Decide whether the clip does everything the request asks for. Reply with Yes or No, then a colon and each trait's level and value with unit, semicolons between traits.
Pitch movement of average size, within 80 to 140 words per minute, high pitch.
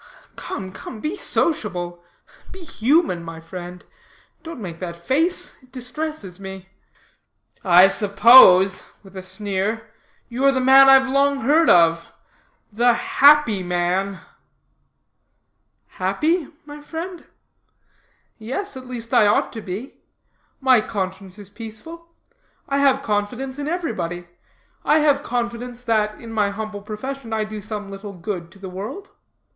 No: wide, 6.0 semitones; slow, 135 wpm; high, 220 Hz